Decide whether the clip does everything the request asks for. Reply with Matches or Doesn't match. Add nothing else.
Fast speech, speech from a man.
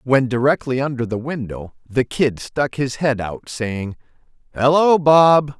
Doesn't match